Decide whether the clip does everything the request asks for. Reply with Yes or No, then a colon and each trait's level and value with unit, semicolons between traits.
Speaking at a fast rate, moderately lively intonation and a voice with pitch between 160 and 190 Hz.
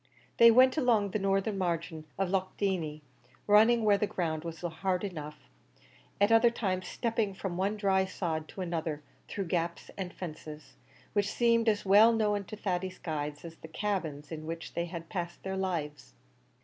No: average, 175 wpm; average, 3.8 semitones; medium, 185 Hz